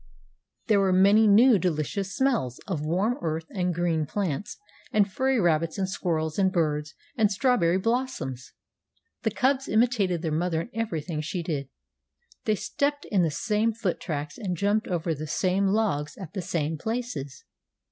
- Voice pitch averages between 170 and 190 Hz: Yes, medium, 185 Hz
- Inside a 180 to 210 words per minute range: No, average, 160 wpm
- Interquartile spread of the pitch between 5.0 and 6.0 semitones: Yes, wide, 5.4 semitones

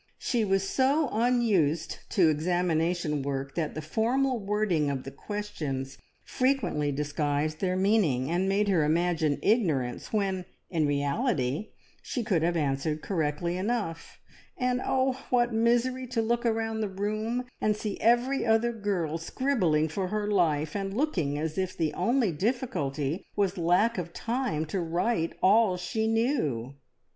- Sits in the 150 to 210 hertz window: Yes, high, 190 Hz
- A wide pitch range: Yes, wide, 6.5 semitones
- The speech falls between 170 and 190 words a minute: No, average, 145 wpm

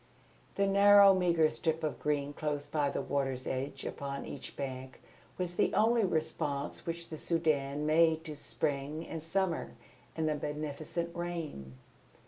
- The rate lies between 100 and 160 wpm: Yes, average, 145 wpm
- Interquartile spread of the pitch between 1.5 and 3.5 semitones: Yes, average, 3.0 semitones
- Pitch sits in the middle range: Yes, medium, 155 Hz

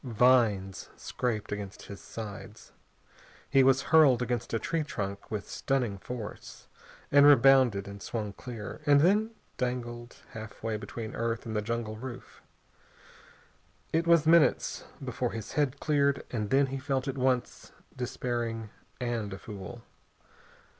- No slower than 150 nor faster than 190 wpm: No, slow, 135 wpm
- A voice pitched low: Yes, low, 120 Hz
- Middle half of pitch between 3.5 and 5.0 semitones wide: Yes, average, 3.9 semitones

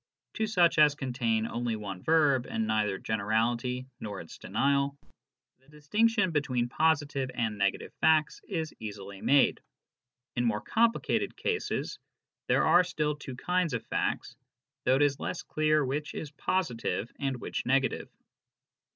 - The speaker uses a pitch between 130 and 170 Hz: Yes, low, 135 Hz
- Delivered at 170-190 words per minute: No, average, 140 wpm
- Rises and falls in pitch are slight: No, average, 5.2 semitones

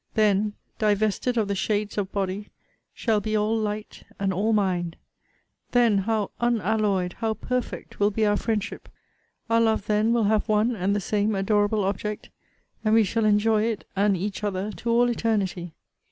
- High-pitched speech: Yes, high, 210 Hz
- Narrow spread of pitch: Yes, narrow, 1.8 semitones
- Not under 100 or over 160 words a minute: No, average, 170 wpm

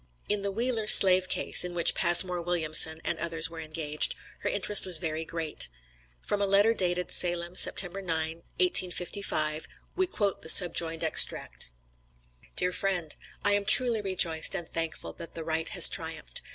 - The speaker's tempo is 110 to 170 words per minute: Yes, average, 160 wpm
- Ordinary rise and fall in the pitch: Yes, average, 3.4 semitones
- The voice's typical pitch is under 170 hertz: No, medium, 175 Hz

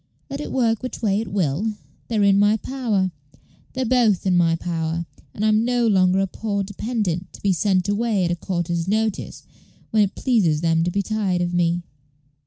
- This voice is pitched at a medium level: No, high, 200 Hz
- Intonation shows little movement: No, average, 3.9 semitones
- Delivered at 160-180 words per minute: No, average, 195 wpm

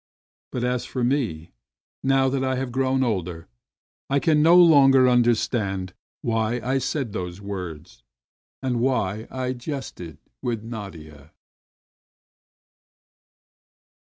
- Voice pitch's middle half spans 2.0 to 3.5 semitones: No, wide, 5.4 semitones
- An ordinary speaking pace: No, slow, 110 wpm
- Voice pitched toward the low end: Yes, low, 120 Hz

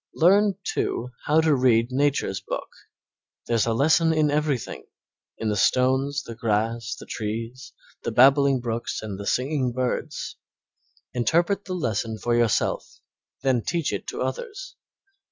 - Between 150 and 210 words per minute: No, average, 140 wpm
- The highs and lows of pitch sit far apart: No, average, 4.9 semitones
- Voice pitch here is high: No, low, 130 Hz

